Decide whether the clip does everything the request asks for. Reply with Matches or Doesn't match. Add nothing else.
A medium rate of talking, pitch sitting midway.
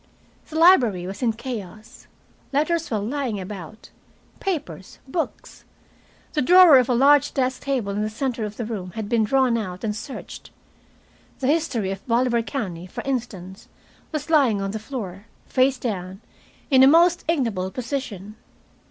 Doesn't match